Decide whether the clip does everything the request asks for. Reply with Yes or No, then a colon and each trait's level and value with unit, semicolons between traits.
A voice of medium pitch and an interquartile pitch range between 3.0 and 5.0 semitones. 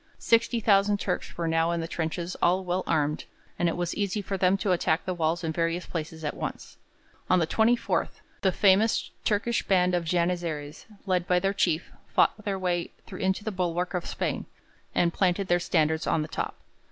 No: medium, 180 Hz; narrow, 2.6 semitones